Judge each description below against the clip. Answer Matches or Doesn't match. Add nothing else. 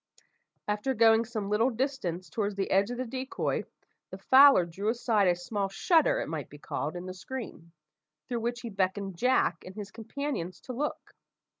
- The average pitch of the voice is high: Matches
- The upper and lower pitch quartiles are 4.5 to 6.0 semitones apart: Matches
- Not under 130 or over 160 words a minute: Doesn't match